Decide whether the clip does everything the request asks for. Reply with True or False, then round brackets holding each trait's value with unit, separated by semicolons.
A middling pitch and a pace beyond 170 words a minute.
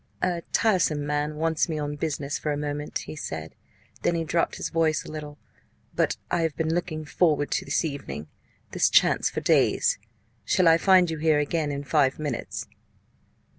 True (155 Hz; 180 wpm)